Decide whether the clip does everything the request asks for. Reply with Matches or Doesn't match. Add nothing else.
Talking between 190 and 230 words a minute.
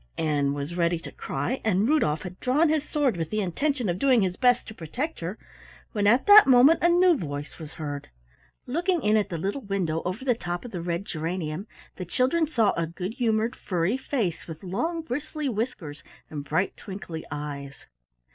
Matches